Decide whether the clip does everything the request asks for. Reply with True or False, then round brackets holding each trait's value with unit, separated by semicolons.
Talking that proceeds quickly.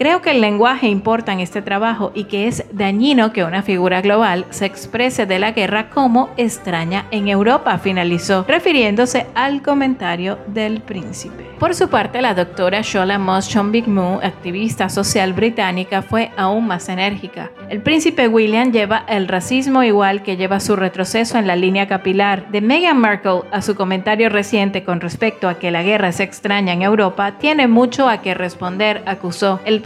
False (175 wpm)